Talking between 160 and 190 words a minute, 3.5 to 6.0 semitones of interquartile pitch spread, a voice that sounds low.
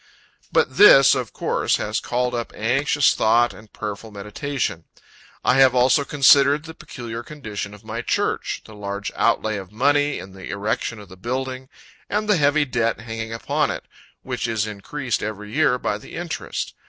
Yes: average, 170 wpm; average, 4.6 semitones; low, 120 Hz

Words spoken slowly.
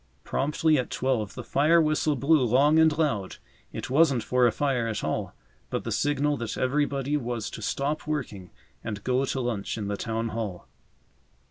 No: average, 175 wpm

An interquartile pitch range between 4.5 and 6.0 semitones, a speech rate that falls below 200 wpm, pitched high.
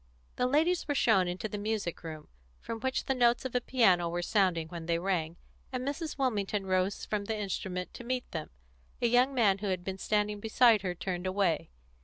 No: average, 5.0 semitones; fast, 205 wpm; high, 205 Hz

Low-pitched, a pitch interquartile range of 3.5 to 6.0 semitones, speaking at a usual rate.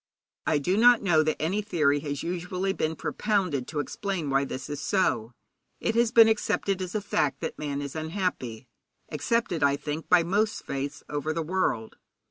No: medium, 160 Hz; wide, 5.4 semitones; average, 180 wpm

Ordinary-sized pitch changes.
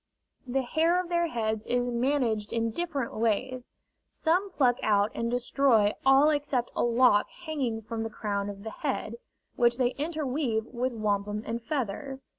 Yes: average, 4.1 semitones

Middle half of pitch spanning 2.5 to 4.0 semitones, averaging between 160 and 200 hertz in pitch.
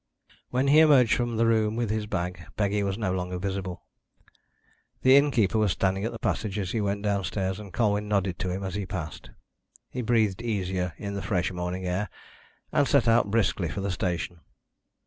No: average, 3.2 semitones; low, 100 Hz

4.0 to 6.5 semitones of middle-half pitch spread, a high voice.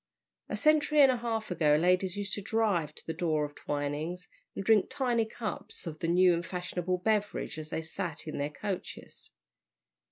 No: average, 5.1 semitones; medium, 180 Hz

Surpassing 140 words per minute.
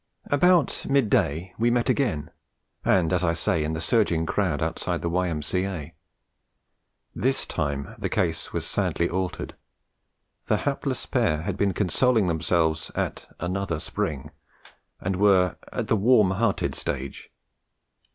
No: slow, 135 wpm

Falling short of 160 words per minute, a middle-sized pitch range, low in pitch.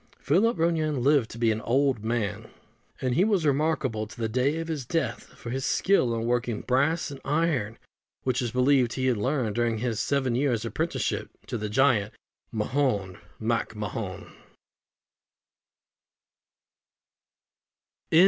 Yes: average, 140 wpm; average, 4.1 semitones; low, 125 Hz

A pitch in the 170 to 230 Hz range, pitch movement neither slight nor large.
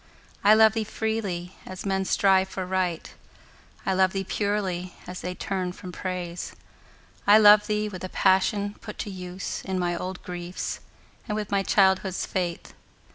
No: high, 190 Hz; narrow, 2.1 semitones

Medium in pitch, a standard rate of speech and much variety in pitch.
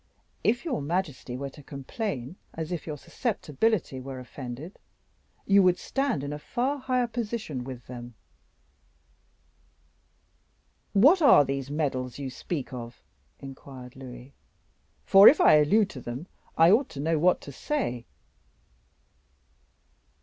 No: medium, 150 Hz; slow, 130 wpm; wide, 7.7 semitones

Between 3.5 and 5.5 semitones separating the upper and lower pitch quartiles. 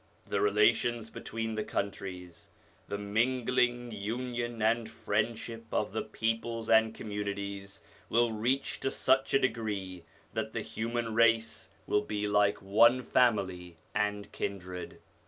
No: narrow, 2.5 semitones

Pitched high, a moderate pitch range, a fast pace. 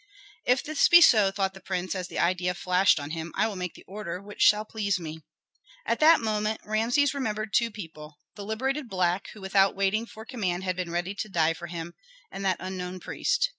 Yes: high, 195 Hz; average, 3.3 semitones; fast, 210 wpm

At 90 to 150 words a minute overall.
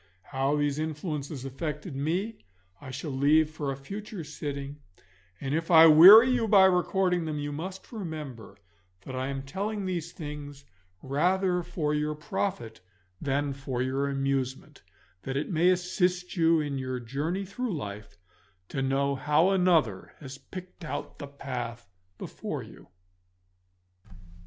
Yes: average, 140 wpm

